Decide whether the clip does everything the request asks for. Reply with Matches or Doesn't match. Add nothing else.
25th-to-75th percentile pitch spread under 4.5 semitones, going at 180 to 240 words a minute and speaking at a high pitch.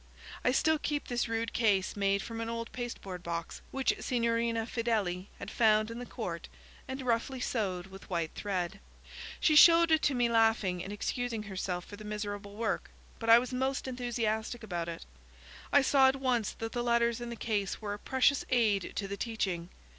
Matches